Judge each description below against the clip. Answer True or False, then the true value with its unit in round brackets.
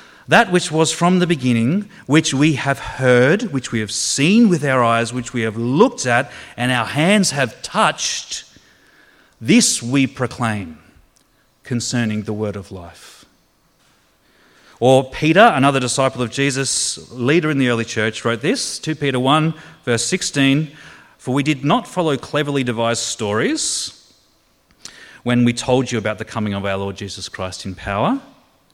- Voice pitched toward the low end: True (125 Hz)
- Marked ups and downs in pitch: False (4.9 semitones)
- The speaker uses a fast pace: False (155 wpm)